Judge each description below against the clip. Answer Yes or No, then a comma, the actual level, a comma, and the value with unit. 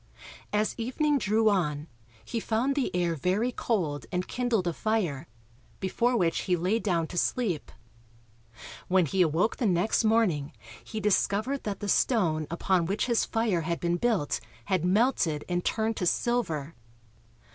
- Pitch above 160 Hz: Yes, high, 190 Hz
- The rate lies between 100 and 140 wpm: No, average, 155 wpm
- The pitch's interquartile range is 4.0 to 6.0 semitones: Yes, average, 4.9 semitones